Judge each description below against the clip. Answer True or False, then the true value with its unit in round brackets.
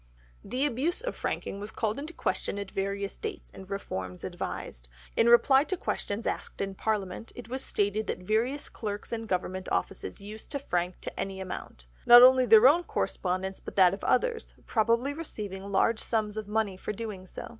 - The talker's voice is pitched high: True (215 Hz)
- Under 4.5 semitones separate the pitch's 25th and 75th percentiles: True (3.9 semitones)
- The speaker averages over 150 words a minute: True (180 wpm)